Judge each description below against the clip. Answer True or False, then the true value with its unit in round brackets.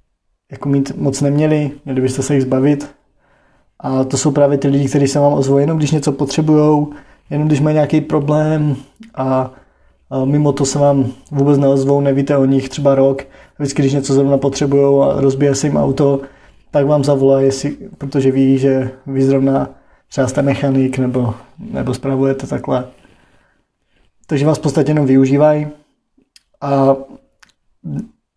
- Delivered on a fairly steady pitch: True (1.4 semitones)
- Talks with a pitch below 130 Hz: False (140 Hz)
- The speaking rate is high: False (150 wpm)